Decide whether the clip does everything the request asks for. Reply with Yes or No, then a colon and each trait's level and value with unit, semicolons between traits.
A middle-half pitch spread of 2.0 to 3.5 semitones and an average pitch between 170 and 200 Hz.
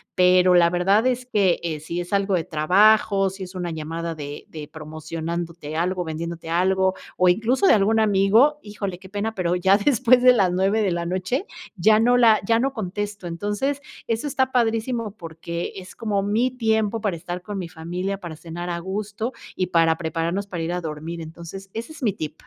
No: average, 4.2 semitones; high, 190 Hz